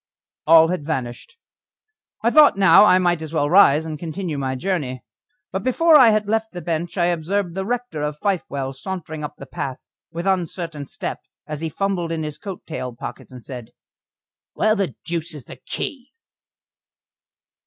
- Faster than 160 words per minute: Yes, average, 175 wpm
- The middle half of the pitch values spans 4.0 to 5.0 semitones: Yes, average, 4.6 semitones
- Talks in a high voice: No, medium, 170 Hz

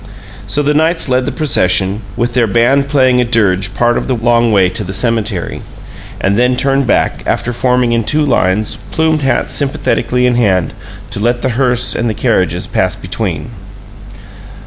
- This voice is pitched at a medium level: No, low, 120 Hz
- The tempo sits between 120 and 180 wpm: Yes, average, 175 wpm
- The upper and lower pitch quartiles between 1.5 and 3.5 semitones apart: Yes, average, 3.2 semitones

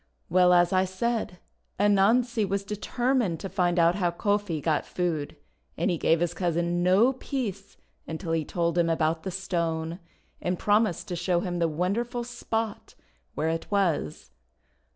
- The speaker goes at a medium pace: Yes, average, 155 wpm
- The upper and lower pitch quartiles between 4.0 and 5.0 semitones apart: No, average, 3.4 semitones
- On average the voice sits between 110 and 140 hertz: No, medium, 180 Hz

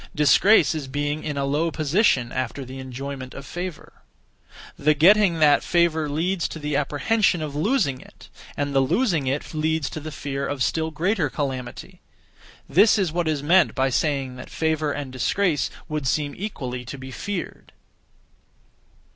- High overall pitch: No, medium, 150 Hz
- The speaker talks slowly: No, average, 165 wpm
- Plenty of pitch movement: No, average, 3.5 semitones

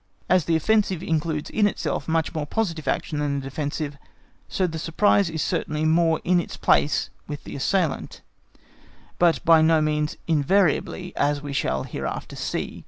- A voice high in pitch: No, medium, 160 Hz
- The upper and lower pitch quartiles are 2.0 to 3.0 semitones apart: Yes, average, 2.7 semitones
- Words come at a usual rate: Yes, average, 165 wpm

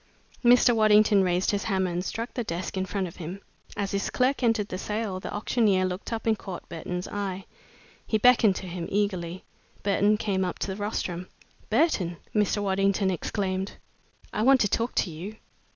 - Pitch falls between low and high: No, high, 200 Hz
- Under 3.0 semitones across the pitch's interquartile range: Yes, narrow, 2.6 semitones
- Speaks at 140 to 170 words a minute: No, average, 185 wpm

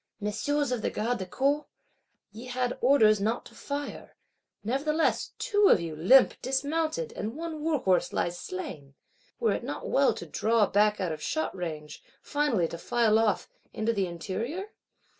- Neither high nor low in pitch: No, high, 230 Hz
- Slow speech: No, average, 165 wpm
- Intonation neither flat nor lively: No, wide, 7.1 semitones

